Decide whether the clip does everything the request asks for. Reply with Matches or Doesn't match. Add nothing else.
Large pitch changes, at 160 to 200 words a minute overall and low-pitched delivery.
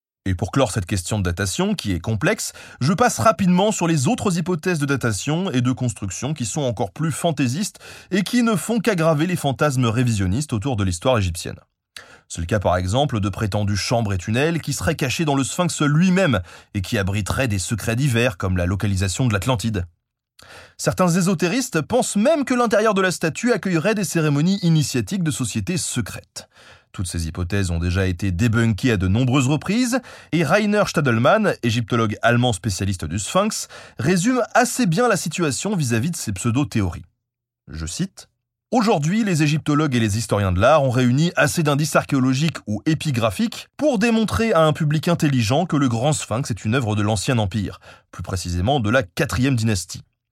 Matches